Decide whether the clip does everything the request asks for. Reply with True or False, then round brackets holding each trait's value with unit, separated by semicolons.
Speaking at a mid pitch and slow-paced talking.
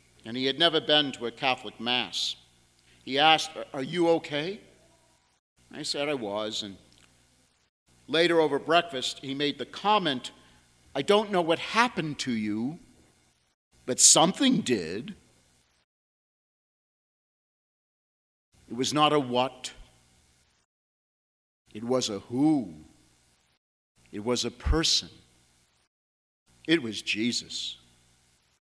False (110 Hz; 110 wpm)